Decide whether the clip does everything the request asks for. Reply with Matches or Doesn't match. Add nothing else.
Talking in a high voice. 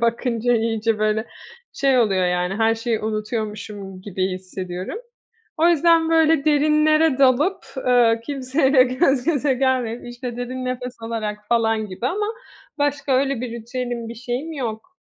Matches